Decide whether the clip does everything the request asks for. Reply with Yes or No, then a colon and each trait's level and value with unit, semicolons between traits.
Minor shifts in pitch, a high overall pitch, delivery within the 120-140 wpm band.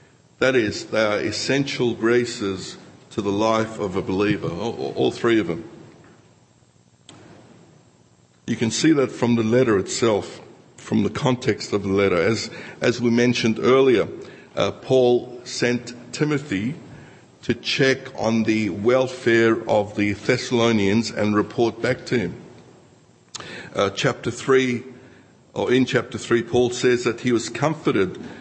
No: narrow, 2.2 semitones; low, 120 Hz; slow, 135 wpm